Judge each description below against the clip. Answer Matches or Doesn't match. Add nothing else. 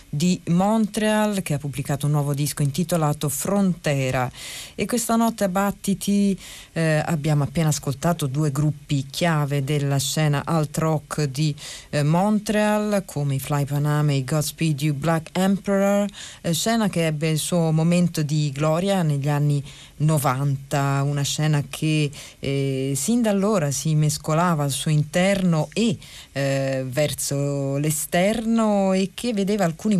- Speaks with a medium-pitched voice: Matches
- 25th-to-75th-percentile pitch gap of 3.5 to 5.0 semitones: Matches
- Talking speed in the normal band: Matches